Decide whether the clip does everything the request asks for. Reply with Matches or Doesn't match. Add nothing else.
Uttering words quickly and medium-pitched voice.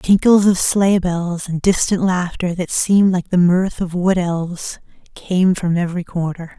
Doesn't match